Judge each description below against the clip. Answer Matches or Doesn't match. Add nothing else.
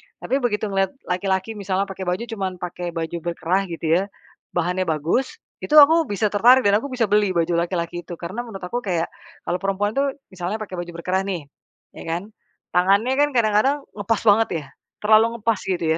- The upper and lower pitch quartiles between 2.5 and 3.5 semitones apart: Doesn't match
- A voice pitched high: Matches